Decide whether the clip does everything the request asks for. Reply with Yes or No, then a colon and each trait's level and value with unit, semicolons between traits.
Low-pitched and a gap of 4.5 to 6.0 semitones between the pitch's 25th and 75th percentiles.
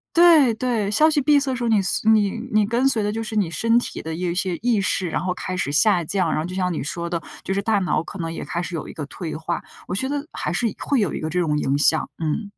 No: high, 195 Hz; average, 5.1 semitones